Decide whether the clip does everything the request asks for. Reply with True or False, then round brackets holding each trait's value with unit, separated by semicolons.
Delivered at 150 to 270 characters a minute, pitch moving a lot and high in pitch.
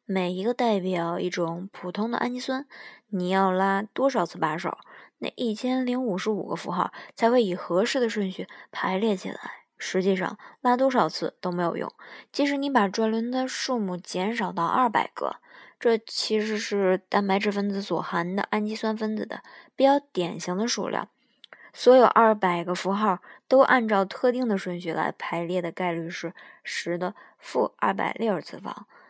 False (260 characters per minute; 4.9 semitones; 205 Hz)